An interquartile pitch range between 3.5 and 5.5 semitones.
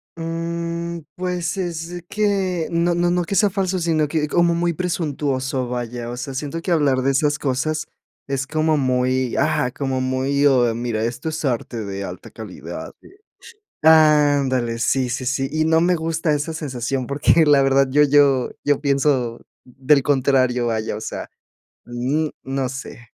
Yes: average, 4.2 semitones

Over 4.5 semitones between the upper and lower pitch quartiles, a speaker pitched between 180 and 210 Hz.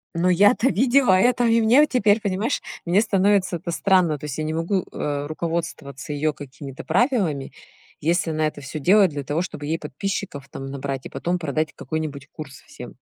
No: average, 5.3 semitones; medium, 165 Hz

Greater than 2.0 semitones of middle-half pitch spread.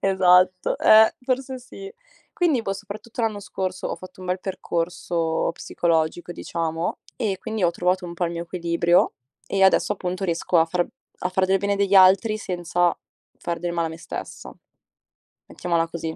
Yes: narrow, 2.6 semitones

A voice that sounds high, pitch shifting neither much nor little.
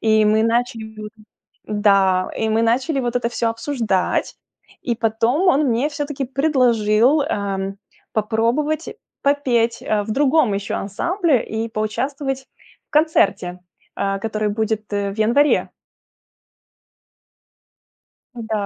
Yes: high, 230 Hz; average, 4.2 semitones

